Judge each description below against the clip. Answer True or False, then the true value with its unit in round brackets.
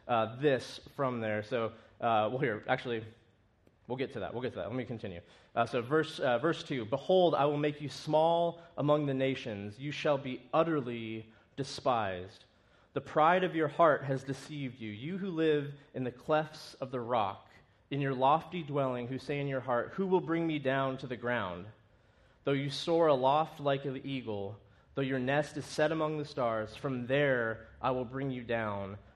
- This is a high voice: False (135 Hz)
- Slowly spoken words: False (200 wpm)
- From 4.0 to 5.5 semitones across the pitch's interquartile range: True (4.5 semitones)